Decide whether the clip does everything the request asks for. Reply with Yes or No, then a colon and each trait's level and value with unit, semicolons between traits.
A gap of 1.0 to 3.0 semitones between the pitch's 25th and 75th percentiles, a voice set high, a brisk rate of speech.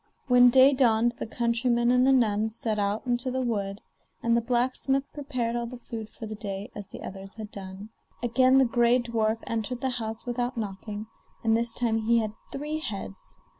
No: narrow, 2.4 semitones; high, 235 Hz; average, 195 wpm